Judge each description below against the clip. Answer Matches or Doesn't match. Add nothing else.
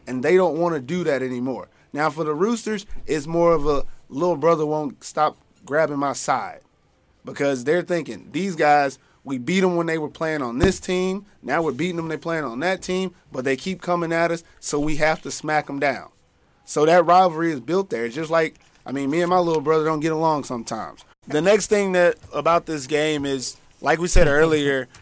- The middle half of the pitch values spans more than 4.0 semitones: Doesn't match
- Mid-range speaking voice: Matches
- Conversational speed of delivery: Doesn't match